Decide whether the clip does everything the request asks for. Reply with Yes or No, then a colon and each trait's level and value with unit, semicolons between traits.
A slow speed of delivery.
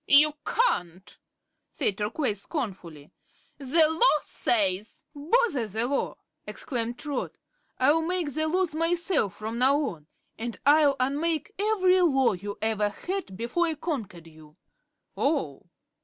Yes: slow, 130 wpm